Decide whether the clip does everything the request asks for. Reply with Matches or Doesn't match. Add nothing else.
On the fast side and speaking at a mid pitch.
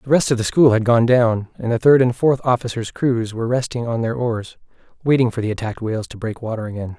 Doesn't match